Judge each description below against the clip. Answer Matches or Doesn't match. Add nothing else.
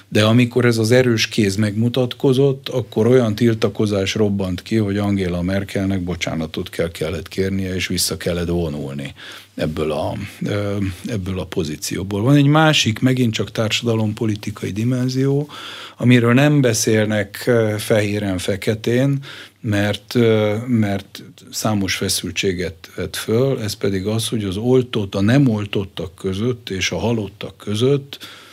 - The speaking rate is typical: Matches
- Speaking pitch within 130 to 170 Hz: Doesn't match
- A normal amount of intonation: Matches